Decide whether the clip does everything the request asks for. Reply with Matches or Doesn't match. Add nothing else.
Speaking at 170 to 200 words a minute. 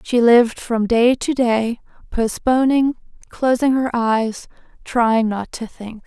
Doesn't match